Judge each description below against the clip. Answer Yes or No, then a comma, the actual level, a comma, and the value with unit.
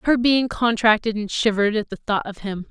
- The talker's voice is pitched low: No, high, 220 Hz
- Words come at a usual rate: No, fast, 220 wpm